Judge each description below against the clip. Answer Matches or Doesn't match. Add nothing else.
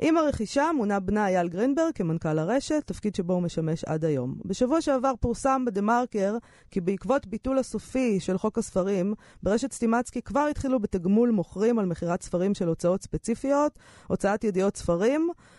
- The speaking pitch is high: Matches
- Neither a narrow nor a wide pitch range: Doesn't match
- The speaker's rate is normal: Doesn't match